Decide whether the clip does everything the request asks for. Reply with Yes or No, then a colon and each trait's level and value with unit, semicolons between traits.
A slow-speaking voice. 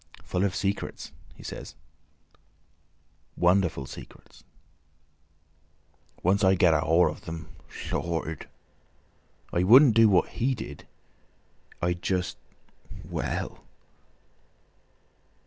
Yes: slow, 85 wpm